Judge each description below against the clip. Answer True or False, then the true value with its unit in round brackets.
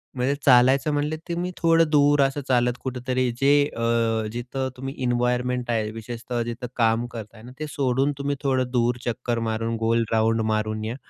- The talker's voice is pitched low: True (125 Hz)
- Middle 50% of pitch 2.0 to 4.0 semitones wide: True (2.8 semitones)